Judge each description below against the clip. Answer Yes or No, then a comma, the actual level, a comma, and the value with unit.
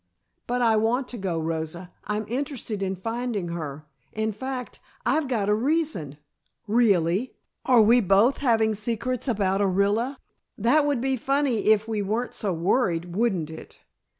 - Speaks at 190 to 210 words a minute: No, average, 155 wpm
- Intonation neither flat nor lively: Yes, average, 4.5 semitones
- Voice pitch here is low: No, high, 220 Hz